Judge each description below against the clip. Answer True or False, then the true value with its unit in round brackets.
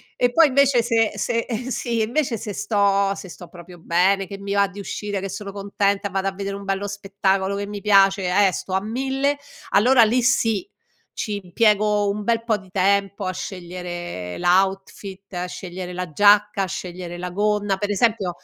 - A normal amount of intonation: False (1.9 semitones)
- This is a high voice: True (200 Hz)